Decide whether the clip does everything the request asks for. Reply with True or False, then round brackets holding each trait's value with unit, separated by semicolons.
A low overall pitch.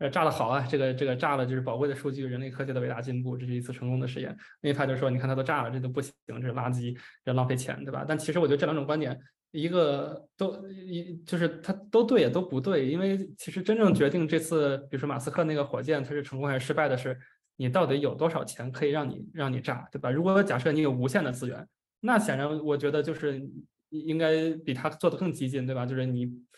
False (145 Hz)